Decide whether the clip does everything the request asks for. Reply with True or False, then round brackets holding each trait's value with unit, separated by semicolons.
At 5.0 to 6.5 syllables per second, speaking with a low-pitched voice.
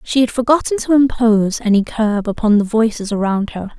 False (5.3 syllables/s; 225 Hz)